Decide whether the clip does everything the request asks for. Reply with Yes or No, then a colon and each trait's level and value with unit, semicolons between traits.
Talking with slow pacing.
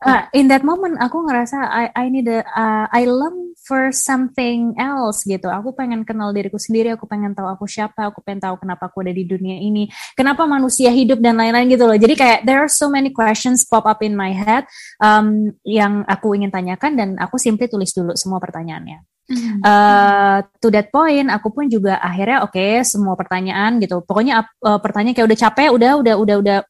No: fast, 205 wpm